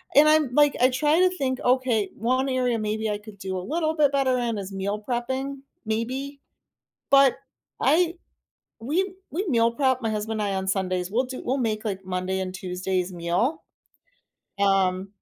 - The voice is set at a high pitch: Yes, high, 235 Hz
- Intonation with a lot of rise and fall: Yes, wide, 5.9 semitones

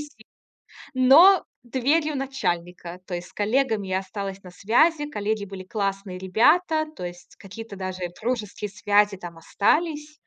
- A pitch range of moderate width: No, wide, 6.3 semitones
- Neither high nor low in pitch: No, high, 210 Hz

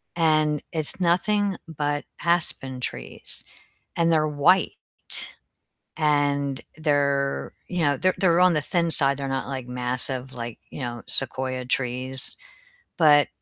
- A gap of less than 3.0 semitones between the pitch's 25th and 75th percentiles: No, average, 3.7 semitones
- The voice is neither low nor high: Yes, medium, 145 Hz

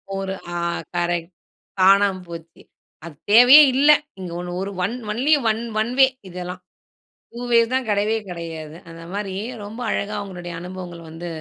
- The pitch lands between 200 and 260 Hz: No, high, 190 Hz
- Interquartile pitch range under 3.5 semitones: No, average, 4.3 semitones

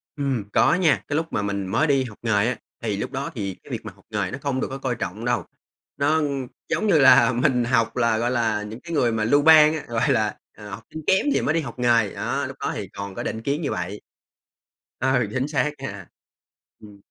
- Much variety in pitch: No, average, 4.8 semitones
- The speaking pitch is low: Yes, low, 125 Hz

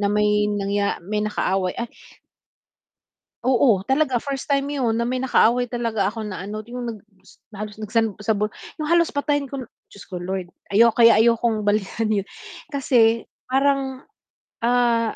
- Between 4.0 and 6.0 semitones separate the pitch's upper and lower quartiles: No, average, 3.5 semitones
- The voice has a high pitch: Yes, high, 230 Hz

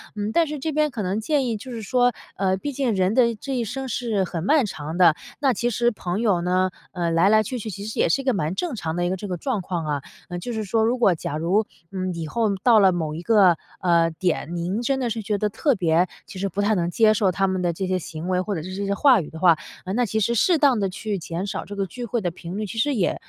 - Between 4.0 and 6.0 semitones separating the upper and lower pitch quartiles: Yes, average, 4.7 semitones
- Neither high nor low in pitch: No, high, 200 Hz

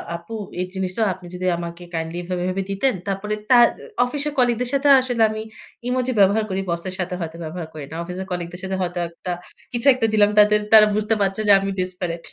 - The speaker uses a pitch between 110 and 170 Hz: No, high, 190 Hz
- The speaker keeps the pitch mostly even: No, average, 4.0 semitones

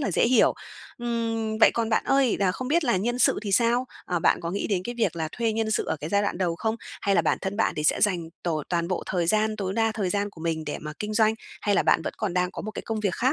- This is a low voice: No, high, 210 Hz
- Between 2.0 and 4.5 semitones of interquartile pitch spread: Yes, average, 4.0 semitones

